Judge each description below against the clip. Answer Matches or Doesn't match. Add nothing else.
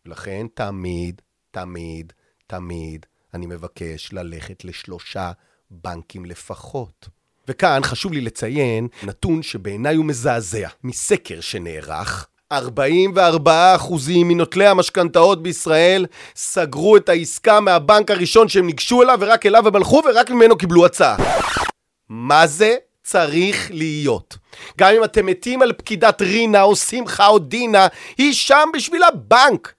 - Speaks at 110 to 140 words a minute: Matches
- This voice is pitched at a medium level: Matches